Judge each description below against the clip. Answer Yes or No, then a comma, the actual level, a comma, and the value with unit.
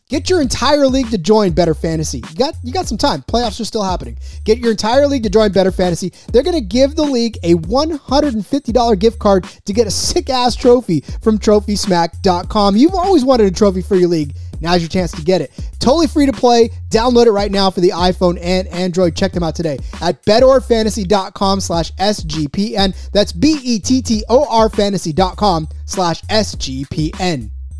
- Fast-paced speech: No, average, 180 wpm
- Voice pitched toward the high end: Yes, high, 210 Hz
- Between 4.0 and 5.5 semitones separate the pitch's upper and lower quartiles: Yes, average, 5.2 semitones